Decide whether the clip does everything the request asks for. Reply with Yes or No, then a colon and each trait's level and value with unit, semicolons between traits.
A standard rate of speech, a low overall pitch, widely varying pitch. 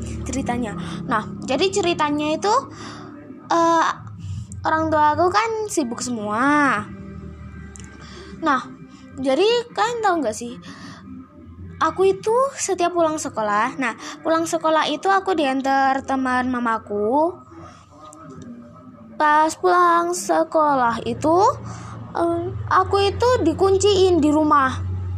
No: average, 100 wpm; very high, 310 Hz; wide, 7.2 semitones